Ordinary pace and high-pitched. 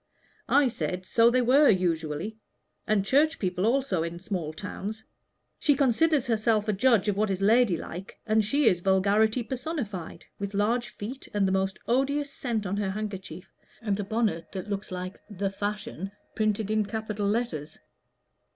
Yes: average, 160 wpm; high, 210 Hz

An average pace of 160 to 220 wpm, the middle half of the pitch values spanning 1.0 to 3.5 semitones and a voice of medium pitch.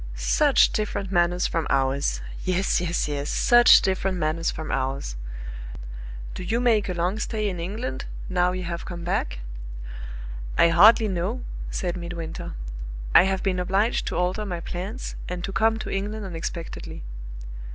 No: average, 150 wpm; average, 3.0 semitones; medium, 180 Hz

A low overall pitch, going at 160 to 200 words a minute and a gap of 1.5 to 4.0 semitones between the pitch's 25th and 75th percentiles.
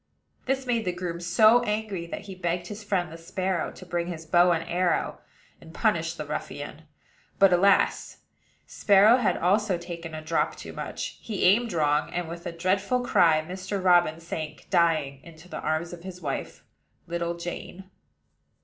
No: medium, 175 Hz; average, 170 wpm; average, 2.7 semitones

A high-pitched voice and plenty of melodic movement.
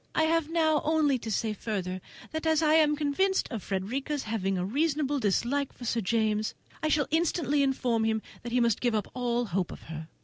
Yes: very high, 250 Hz; wide, 5.9 semitones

